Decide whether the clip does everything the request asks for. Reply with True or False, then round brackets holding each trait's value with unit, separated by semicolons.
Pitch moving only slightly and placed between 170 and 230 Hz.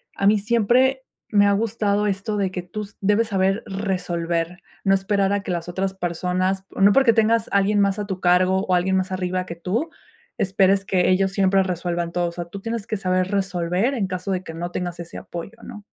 True (2.2 semitones; 190 Hz)